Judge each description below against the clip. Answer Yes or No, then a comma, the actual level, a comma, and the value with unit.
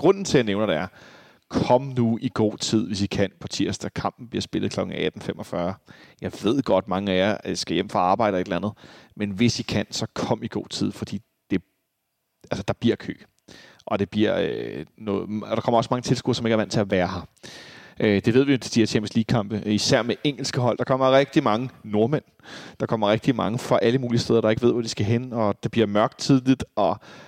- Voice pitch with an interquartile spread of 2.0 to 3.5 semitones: Yes, average, 3.2 semitones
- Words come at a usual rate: No, fast, 240 wpm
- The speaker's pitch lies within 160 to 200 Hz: No, low, 115 Hz